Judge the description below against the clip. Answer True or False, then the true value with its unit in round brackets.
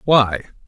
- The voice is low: True (120 Hz)